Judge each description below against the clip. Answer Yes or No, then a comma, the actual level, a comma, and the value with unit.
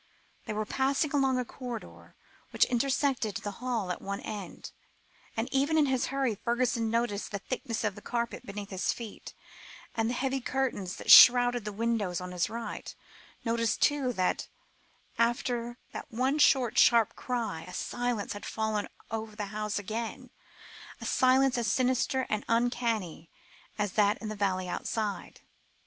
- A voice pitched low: No, high, 230 Hz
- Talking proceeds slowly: No, average, 160 wpm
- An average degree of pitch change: Yes, average, 3.4 semitones